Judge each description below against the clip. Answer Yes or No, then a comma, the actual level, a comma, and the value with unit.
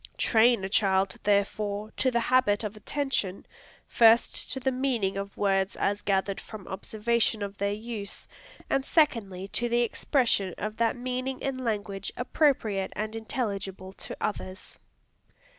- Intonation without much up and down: No, average, 3.5 semitones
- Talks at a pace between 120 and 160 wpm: Yes, average, 140 wpm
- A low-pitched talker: No, high, 215 Hz